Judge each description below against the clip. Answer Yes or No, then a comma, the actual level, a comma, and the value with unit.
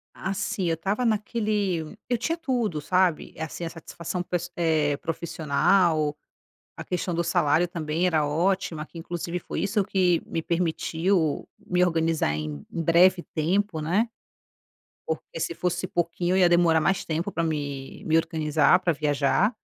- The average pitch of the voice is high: No, medium, 170 Hz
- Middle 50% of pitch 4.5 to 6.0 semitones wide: No, average, 2.8 semitones